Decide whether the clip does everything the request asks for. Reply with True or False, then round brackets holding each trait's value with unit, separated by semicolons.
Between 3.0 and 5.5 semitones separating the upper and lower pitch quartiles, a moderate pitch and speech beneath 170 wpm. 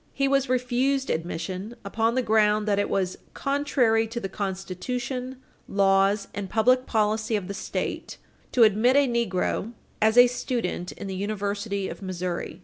False (4.1 semitones; 215 Hz; 155 wpm)